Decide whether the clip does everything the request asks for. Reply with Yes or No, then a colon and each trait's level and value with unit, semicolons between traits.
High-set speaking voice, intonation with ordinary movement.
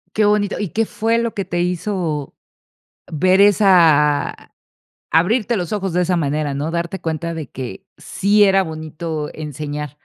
No: medium, 170 Hz; average, 4.6 semitones